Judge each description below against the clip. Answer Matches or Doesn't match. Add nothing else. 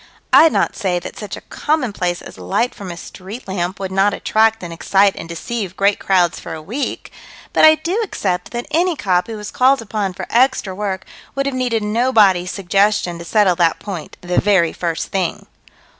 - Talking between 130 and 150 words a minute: Doesn't match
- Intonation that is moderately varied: Matches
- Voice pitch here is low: Doesn't match